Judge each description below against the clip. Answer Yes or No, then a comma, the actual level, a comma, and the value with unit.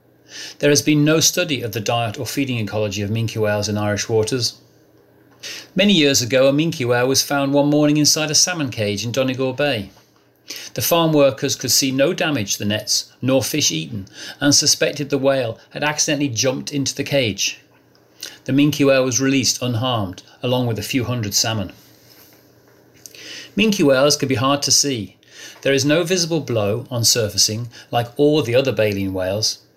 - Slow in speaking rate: No, average, 180 wpm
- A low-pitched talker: Yes, low, 130 Hz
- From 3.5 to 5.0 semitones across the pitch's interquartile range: Yes, average, 4.3 semitones